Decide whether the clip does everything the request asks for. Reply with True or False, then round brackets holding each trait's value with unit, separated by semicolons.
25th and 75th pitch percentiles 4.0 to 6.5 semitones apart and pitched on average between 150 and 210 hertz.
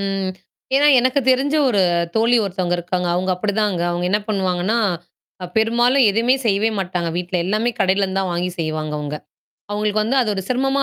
True (4.3 semitones; 200 Hz)